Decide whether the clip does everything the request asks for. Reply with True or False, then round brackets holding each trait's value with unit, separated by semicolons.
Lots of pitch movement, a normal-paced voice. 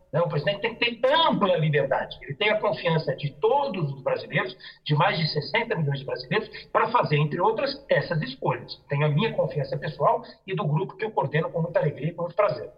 False (6.7 semitones; 220 wpm)